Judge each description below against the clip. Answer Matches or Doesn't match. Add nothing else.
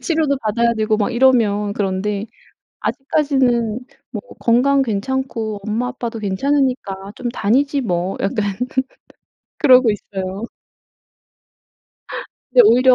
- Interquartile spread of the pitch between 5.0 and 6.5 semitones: Doesn't match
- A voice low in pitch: Doesn't match